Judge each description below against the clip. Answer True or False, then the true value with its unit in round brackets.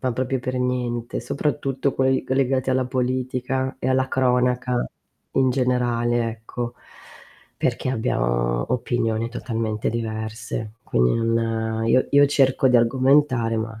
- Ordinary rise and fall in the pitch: False (2.3 semitones)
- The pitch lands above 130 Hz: False (125 Hz)